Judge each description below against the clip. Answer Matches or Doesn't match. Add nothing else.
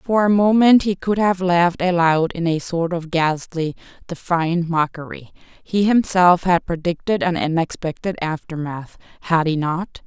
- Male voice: Doesn't match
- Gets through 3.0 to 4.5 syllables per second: Matches